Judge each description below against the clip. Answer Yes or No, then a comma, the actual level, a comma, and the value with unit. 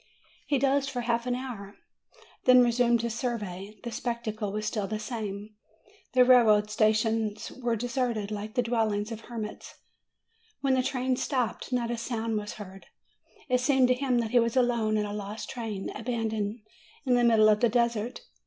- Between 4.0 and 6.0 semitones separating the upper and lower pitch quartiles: No, narrow, 2.6 semitones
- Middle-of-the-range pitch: No, high, 230 Hz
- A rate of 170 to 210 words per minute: Yes, average, 180 wpm